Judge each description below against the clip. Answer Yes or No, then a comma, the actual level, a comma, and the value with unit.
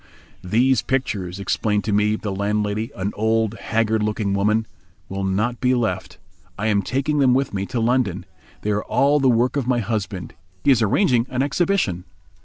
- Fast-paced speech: No, average, 180 wpm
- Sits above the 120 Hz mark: No, low, 110 Hz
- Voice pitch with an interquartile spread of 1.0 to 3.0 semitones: No, average, 3.8 semitones